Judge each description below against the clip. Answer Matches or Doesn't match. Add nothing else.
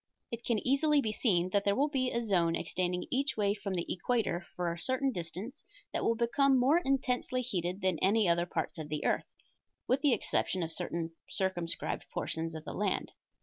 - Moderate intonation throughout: Doesn't match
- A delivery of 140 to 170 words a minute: Doesn't match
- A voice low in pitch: Doesn't match